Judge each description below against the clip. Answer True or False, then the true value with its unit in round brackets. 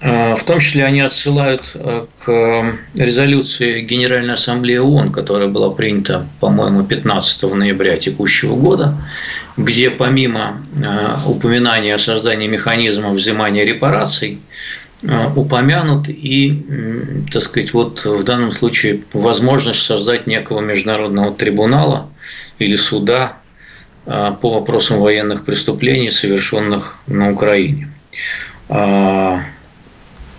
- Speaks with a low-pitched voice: True (115 Hz)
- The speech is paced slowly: True (95 wpm)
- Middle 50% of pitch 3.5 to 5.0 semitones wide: True (4.0 semitones)